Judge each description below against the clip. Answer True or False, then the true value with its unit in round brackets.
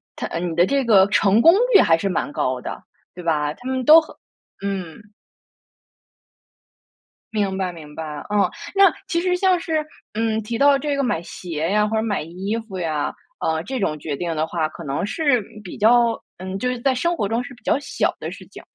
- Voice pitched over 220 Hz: False (205 Hz)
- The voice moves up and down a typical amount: False (7.1 semitones)